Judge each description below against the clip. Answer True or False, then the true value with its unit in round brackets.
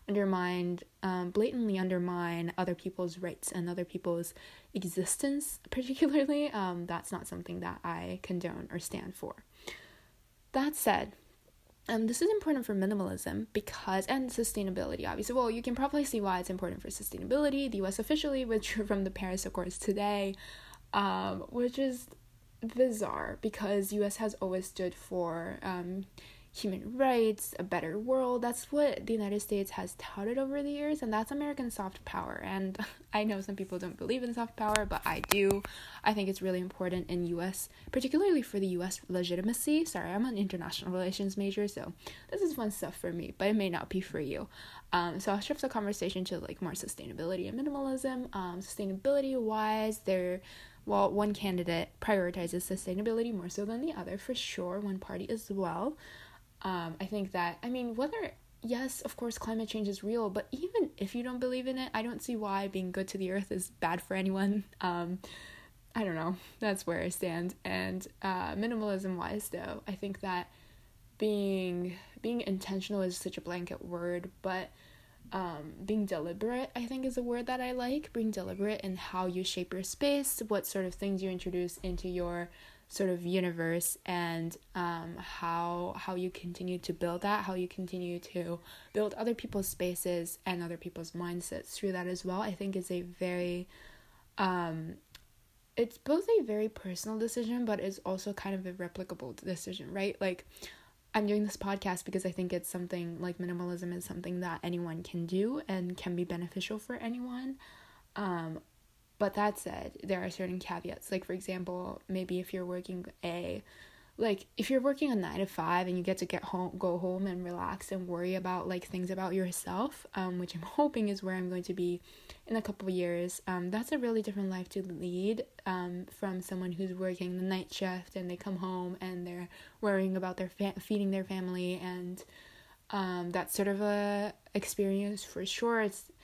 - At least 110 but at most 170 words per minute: False (185 wpm)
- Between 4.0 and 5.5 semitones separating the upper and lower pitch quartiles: False (3.1 semitones)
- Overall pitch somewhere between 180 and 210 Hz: True (190 Hz)